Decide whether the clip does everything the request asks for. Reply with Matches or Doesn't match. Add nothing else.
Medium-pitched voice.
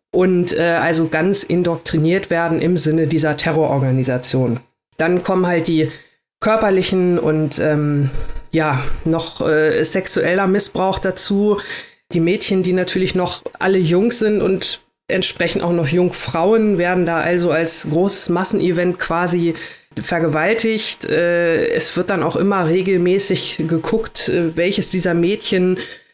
Matches